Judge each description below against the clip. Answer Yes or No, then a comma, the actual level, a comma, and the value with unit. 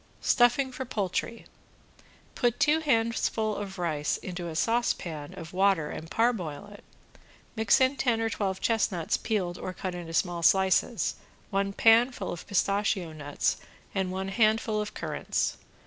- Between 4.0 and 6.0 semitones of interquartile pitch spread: Yes, average, 4.3 semitones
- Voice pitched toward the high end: Yes, high, 200 Hz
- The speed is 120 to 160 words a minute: Yes, average, 145 wpm